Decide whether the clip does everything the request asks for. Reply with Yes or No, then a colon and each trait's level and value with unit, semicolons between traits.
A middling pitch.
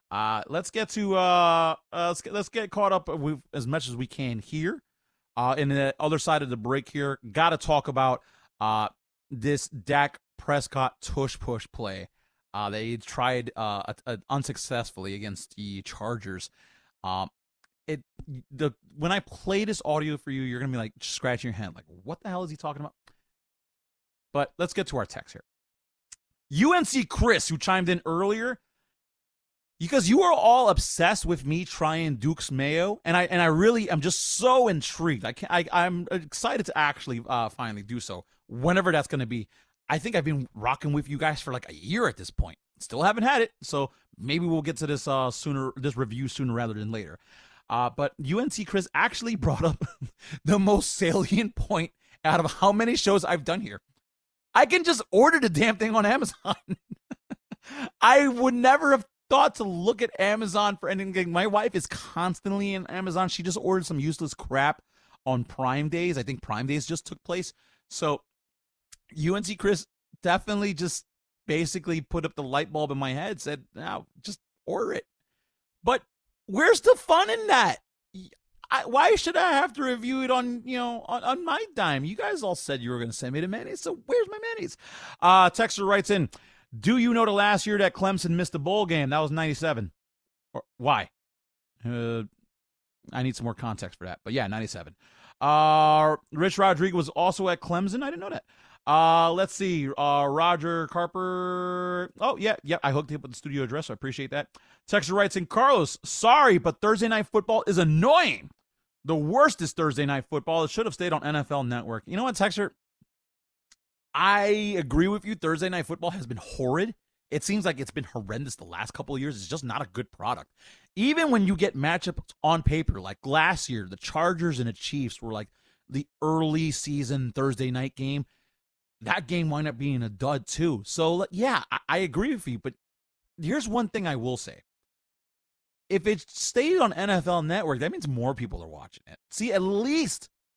Yes: medium, 160 Hz